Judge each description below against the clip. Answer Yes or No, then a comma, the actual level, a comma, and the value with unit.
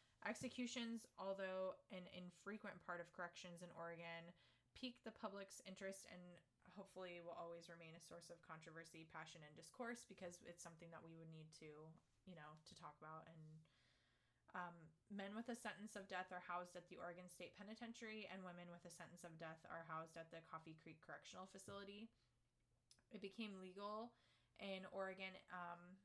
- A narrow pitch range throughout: No, average, 3.1 semitones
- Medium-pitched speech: Yes, medium, 175 Hz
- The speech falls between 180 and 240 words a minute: No, average, 170 wpm